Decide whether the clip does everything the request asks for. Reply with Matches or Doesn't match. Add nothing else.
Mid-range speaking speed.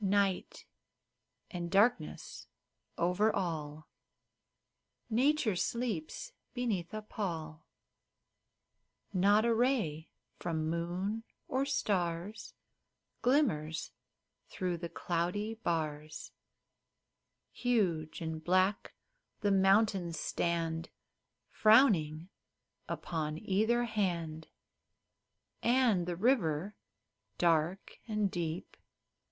Doesn't match